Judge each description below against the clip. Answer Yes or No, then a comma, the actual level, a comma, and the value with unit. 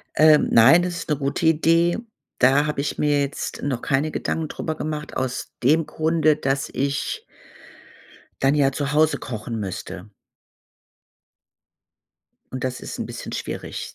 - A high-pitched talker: No, medium, 145 Hz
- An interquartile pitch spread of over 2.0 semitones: Yes, average, 2.7 semitones